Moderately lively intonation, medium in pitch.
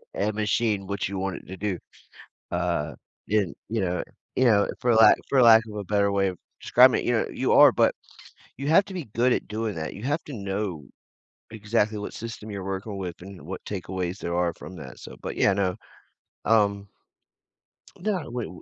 No: average, 3.0 semitones; low, 100 Hz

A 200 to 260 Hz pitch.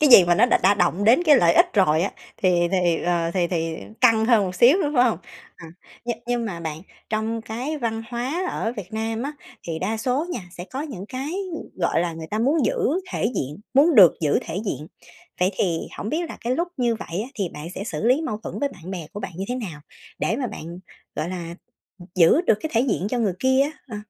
Yes: high, 215 Hz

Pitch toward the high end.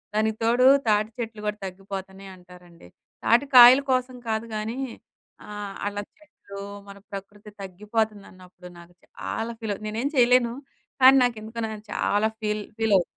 Yes: high, 215 Hz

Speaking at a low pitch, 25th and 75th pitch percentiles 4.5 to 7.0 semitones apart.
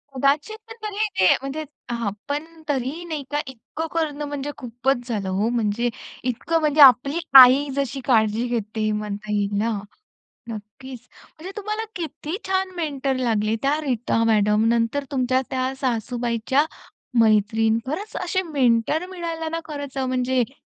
No: very high, 260 Hz; average, 4.9 semitones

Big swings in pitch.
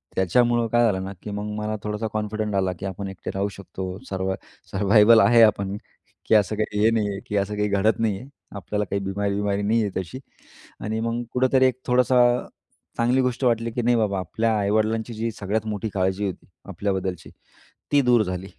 No: narrow, 2.6 semitones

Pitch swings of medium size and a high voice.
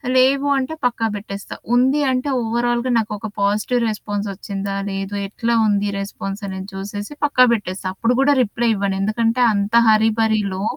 Yes: average, 3.2 semitones; high, 215 Hz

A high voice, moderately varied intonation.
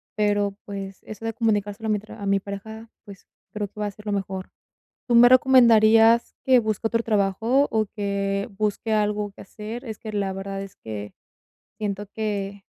No: high, 210 Hz; narrow, 2.0 semitones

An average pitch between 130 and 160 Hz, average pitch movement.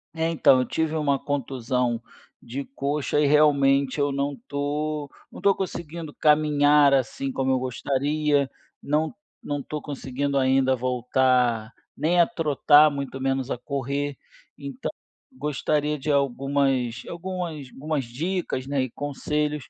No: medium, 140 Hz; narrow, 2.2 semitones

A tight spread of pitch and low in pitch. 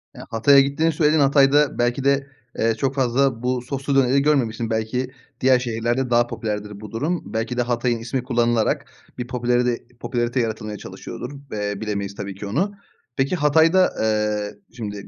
No: average, 3.5 semitones; low, 120 Hz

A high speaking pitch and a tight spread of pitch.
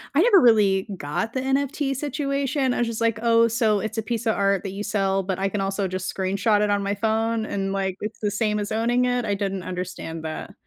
No: high, 210 Hz; average, 3.4 semitones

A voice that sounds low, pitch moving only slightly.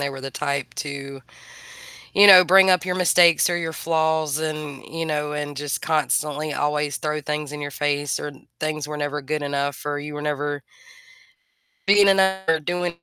No: medium, 150 Hz; narrow, 2.0 semitones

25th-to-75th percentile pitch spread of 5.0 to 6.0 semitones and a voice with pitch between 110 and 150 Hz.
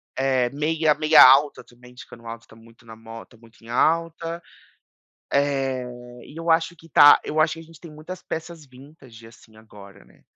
Yes: wide, 5.5 semitones; medium, 140 Hz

